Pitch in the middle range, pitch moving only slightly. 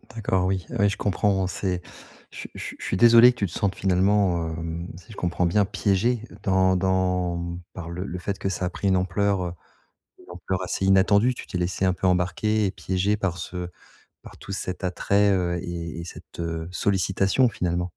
No: very low, 95 Hz; narrow, 2.1 semitones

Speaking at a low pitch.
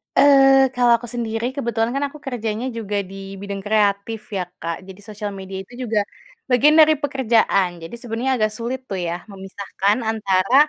No: high, 225 Hz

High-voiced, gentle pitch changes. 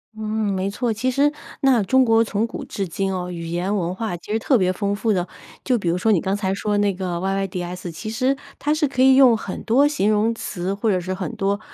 No: high, 205 Hz; average, 3.8 semitones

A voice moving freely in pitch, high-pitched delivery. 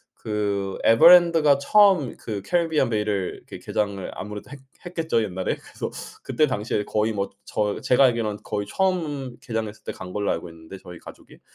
No: wide, 6.3 semitones; low, 110 Hz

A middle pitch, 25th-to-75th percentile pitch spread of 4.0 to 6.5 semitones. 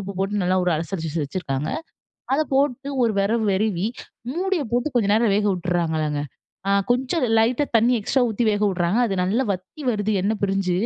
No: high, 200 Hz; average, 5.0 semitones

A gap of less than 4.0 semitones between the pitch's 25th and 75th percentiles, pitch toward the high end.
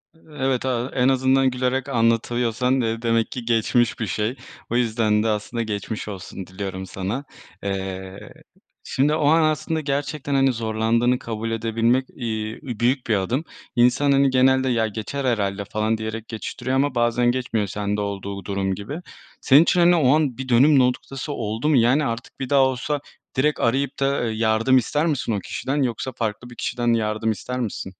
No: average, 3.3 semitones; low, 120 Hz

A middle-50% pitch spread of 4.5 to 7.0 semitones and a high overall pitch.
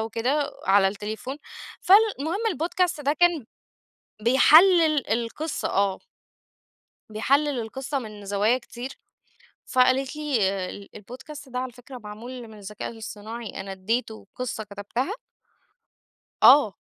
Yes: average, 5.1 semitones; high, 245 Hz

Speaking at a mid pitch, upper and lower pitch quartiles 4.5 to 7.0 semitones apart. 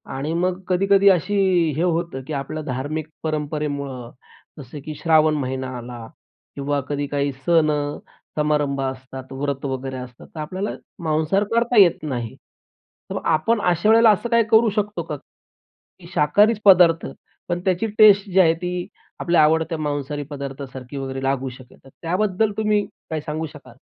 Yes: medium, 155 Hz; average, 4.8 semitones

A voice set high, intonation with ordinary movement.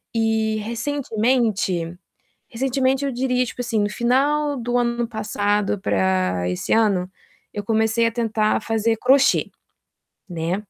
Yes: high, 225 Hz; average, 3.2 semitones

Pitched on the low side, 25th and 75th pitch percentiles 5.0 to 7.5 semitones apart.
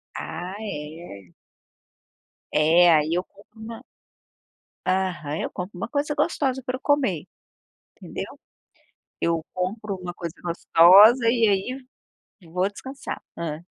No: medium, 185 Hz; wide, 5.5 semitones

